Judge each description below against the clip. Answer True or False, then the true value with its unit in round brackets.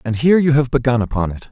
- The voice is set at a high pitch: False (125 Hz)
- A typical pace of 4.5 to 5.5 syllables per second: False (7.1 syllables/s)